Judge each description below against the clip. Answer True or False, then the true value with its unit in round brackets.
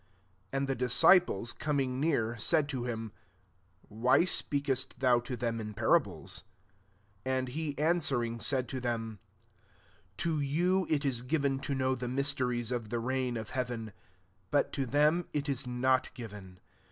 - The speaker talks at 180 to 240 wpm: False (170 wpm)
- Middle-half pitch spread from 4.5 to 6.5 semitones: False (3.3 semitones)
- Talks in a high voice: False (130 Hz)